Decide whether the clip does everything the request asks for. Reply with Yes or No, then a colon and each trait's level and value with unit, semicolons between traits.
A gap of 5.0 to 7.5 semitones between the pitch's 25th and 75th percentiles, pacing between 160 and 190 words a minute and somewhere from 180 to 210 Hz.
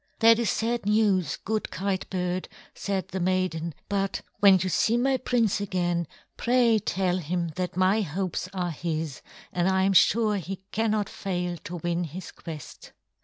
No: average, 3.0 semitones; average, 165 wpm; high, 190 Hz